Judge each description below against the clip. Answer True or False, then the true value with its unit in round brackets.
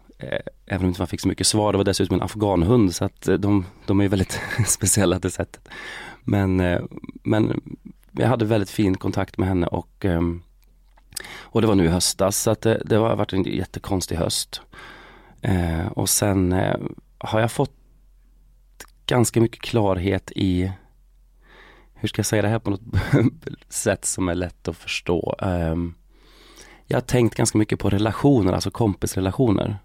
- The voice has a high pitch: False (100 Hz)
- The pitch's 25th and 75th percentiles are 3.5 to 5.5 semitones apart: False (3.1 semitones)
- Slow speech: False (160 wpm)